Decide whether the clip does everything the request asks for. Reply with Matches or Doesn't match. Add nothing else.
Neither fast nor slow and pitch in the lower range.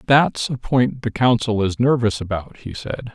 Matches